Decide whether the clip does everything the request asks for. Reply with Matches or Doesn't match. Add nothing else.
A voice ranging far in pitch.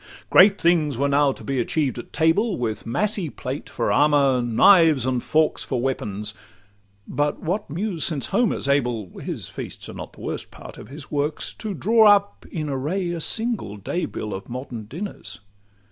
Matches